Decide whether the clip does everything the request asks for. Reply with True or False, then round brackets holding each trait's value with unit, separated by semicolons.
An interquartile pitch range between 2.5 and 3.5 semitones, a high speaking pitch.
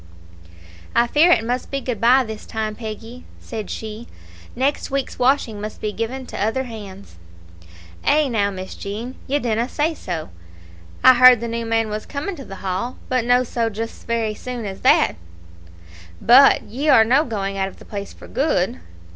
True (3.2 semitones; 230 Hz)